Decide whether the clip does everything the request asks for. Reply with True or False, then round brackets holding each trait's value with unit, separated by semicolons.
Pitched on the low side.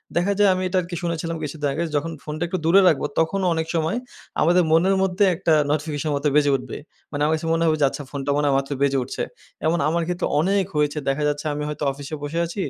False (160 Hz)